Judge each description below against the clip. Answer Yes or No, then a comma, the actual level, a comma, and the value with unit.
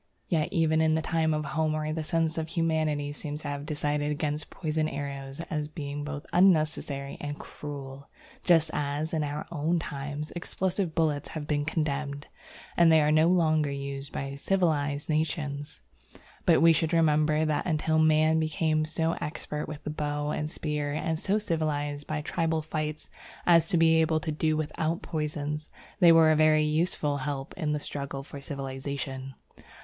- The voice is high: No, medium, 155 Hz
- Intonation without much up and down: Yes, narrow, 1.6 semitones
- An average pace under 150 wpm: No, average, 165 wpm